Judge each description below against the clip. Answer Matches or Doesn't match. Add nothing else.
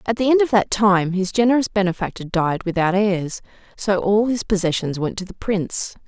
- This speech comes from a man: Doesn't match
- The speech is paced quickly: Doesn't match